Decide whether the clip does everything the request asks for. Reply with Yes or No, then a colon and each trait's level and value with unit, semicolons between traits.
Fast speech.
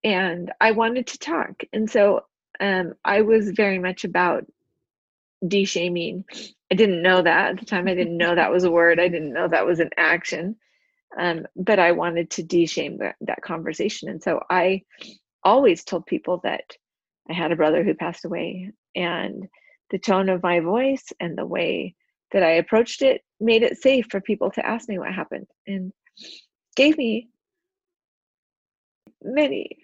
No: average, 175 wpm